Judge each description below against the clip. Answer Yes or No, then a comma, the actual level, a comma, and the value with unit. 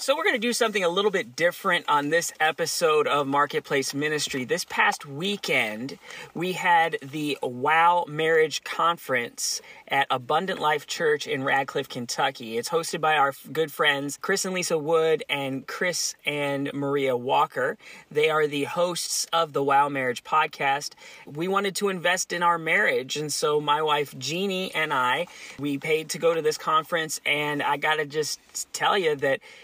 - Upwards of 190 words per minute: No, average, 170 wpm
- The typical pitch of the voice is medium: Yes, medium, 155 Hz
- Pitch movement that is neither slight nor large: Yes, average, 4.2 semitones